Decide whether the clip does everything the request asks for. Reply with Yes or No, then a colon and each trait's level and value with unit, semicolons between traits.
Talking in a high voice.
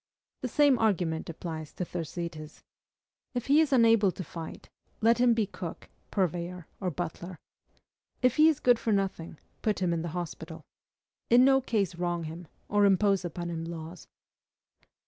No: medium, 180 Hz